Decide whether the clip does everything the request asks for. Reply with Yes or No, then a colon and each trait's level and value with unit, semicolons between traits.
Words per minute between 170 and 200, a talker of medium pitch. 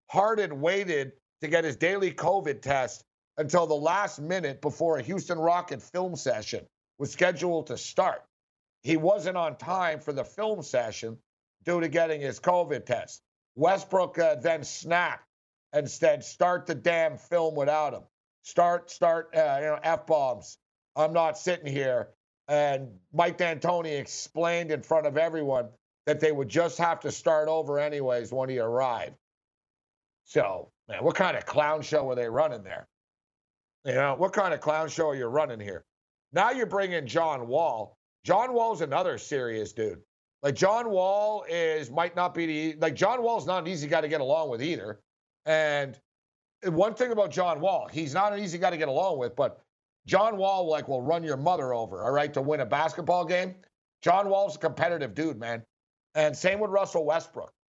Yes: average, 180 wpm; medium, 165 Hz